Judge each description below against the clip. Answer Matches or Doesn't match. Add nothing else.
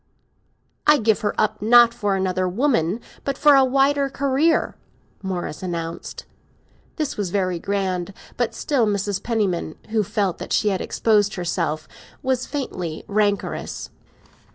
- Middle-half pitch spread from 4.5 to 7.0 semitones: Matches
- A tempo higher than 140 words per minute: Doesn't match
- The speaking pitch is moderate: Doesn't match